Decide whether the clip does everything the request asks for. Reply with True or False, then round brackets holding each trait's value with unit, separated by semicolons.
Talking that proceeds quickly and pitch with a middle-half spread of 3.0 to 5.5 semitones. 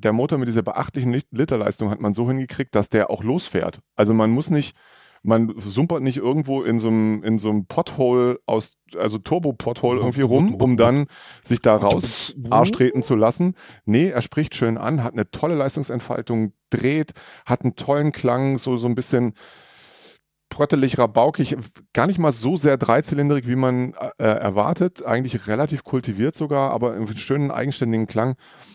False (175 wpm; 3.6 semitones)